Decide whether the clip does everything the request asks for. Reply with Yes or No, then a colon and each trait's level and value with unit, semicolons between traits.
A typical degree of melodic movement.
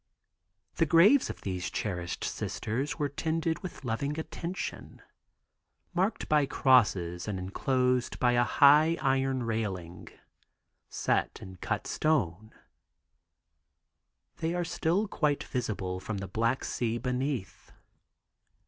No: wide, 7.4 semitones